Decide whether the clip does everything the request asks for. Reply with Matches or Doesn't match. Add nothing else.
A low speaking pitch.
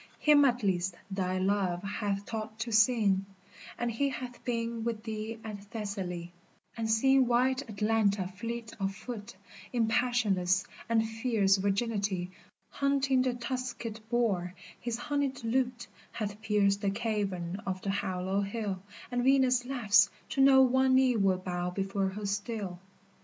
Doesn't match